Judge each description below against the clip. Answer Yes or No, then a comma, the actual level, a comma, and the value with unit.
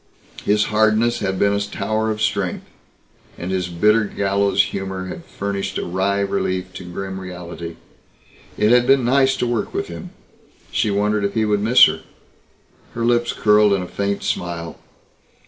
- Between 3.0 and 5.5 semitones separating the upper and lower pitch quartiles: No, narrow, 2.4 semitones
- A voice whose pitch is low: Yes, low, 100 Hz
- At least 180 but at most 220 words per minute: No, average, 165 wpm